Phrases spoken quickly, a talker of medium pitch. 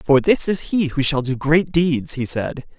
Yes: fast, 235 wpm; medium, 150 Hz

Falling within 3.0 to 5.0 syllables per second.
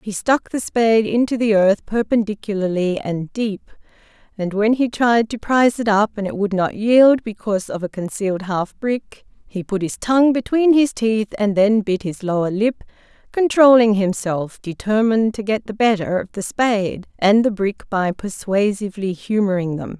Yes: 4.8 syllables/s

